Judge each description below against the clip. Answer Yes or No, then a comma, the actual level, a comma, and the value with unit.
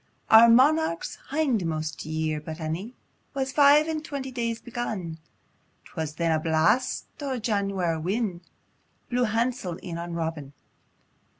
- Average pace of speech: No, slow, 125 wpm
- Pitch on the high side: Yes, high, 200 Hz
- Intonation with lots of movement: Yes, wide, 7.5 semitones